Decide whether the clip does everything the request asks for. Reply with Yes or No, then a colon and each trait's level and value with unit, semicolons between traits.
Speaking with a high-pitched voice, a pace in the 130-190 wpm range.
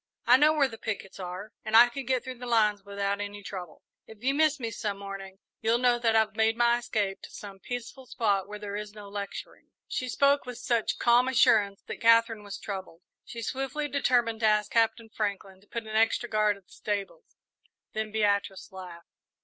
No: high, 220 Hz; fast, 205 wpm